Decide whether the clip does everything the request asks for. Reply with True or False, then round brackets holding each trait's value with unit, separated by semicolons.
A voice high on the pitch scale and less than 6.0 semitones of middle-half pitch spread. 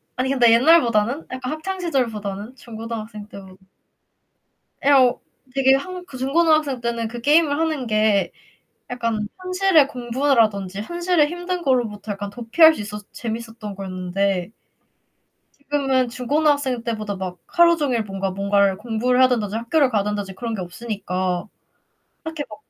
True (235 Hz; 5.4 semitones)